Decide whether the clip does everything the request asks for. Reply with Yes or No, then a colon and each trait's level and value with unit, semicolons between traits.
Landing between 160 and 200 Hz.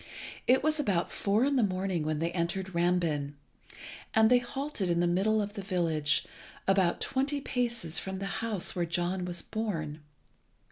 Yes: high, 190 Hz